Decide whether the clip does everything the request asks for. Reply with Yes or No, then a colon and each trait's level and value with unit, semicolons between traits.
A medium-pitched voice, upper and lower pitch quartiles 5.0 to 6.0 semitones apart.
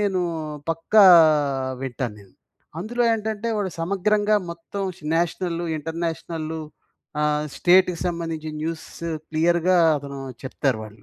No: medium, 170 Hz; average, 3.3 semitones